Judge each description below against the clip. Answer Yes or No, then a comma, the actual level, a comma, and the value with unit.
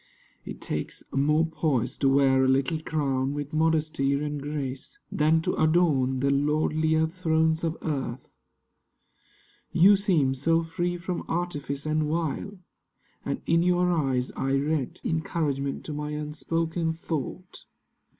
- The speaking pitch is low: No, medium, 155 Hz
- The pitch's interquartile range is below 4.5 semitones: Yes, average, 2.8 semitones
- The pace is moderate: No, slow, 130 wpm